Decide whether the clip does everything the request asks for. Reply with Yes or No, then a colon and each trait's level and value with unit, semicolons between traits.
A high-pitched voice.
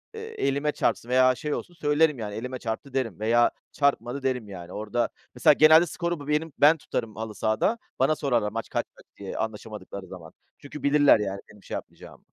No: low, 130 Hz